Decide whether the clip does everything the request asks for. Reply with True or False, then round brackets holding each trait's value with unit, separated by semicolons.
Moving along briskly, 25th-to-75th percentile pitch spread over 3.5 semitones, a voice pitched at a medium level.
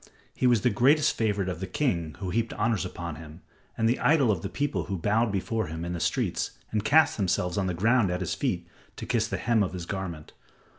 False (235 wpm; 4.5 semitones; 100 Hz)